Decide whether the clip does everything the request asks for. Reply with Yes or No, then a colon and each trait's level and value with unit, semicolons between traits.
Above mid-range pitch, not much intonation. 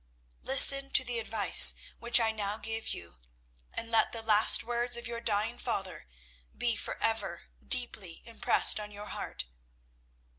Yes: high, 225 Hz; narrow, 2.3 semitones